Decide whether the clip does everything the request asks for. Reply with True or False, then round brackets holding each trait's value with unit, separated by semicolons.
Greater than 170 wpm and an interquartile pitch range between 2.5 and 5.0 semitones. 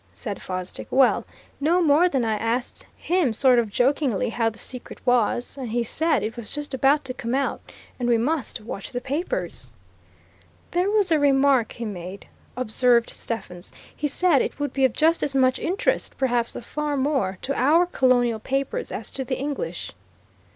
True (180 wpm; 3.9 semitones)